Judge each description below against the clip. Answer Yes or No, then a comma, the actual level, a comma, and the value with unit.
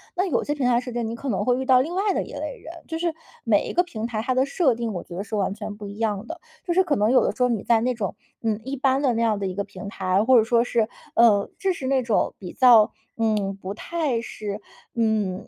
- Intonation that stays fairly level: No, average, 4.0 semitones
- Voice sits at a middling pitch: No, high, 230 Hz